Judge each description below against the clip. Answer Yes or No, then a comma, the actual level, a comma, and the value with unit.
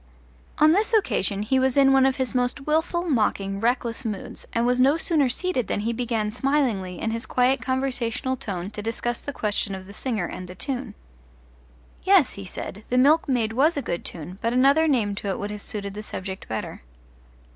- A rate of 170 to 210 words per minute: Yes, average, 200 wpm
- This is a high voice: Yes, high, 240 Hz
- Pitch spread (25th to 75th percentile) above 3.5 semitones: Yes, average, 4.8 semitones